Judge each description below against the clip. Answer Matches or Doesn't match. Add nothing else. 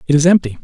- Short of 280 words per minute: Doesn't match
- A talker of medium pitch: Matches